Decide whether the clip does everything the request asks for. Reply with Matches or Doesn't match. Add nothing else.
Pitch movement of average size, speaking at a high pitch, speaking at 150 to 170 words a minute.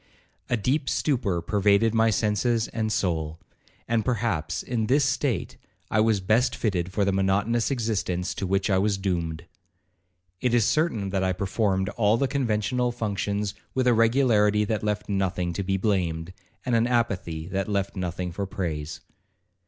Doesn't match